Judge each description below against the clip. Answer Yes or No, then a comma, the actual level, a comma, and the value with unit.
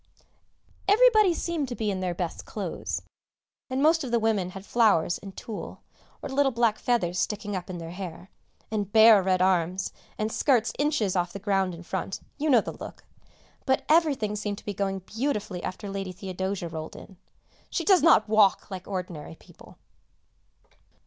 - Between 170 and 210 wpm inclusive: Yes, average, 175 wpm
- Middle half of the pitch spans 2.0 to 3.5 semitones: No, average, 4.6 semitones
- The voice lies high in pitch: Yes, high, 205 Hz